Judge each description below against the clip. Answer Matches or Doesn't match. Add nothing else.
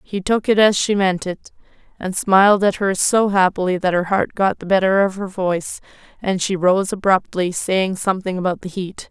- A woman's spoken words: Matches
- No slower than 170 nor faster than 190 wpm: Doesn't match